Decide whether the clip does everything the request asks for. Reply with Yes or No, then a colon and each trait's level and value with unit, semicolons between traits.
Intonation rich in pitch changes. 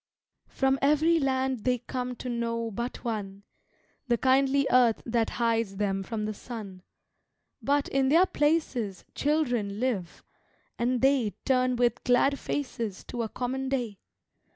No: average, 3.0 semitones